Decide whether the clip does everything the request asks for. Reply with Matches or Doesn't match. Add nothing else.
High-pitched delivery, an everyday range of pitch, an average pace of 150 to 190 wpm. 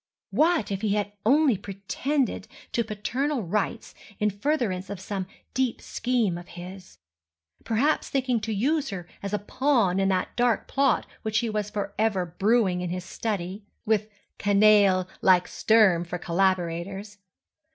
Doesn't match